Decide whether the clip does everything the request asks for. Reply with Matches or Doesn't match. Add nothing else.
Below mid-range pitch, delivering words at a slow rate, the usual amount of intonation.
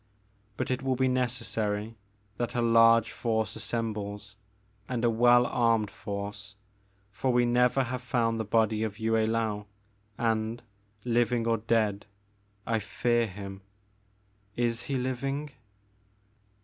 Doesn't match